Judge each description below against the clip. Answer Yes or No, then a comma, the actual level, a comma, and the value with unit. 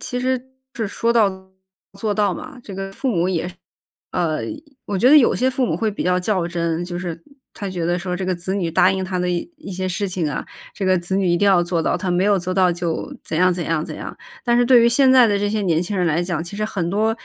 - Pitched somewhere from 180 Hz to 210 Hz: Yes, medium, 185 Hz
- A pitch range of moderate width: Yes, average, 3.3 semitones